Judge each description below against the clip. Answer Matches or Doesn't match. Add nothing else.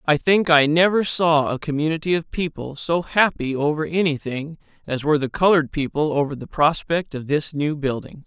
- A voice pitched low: Doesn't match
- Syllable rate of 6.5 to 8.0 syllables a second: Doesn't match